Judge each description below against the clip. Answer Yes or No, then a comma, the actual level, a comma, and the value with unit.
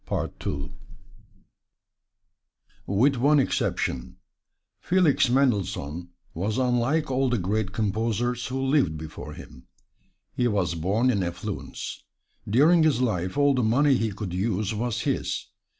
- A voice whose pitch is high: No, low, 115 Hz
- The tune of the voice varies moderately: No, wide, 5.7 semitones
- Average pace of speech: No, slow, 120 wpm